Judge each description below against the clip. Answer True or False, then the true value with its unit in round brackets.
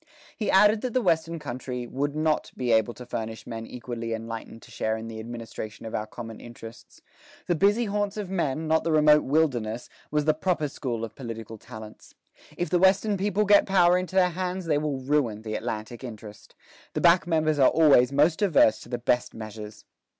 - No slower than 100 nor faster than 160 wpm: False (195 wpm)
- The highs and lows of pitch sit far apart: True (7.2 semitones)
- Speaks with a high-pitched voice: False (140 Hz)